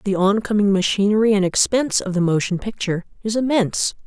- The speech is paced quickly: No, average, 160 wpm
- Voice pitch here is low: No, high, 205 Hz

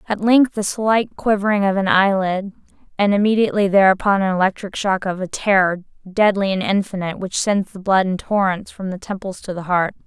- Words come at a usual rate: Yes, average, 190 wpm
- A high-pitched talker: Yes, high, 195 Hz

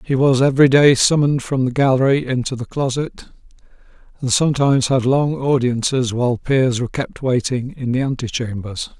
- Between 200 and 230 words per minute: No, average, 160 wpm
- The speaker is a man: Yes, male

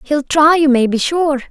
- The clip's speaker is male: No, female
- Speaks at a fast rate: Yes, fast, 240 wpm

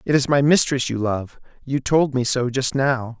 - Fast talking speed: Yes, fast, 225 wpm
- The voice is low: Yes, low, 130 Hz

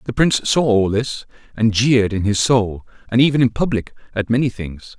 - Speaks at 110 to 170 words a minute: No, fast, 205 wpm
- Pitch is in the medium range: No, low, 115 Hz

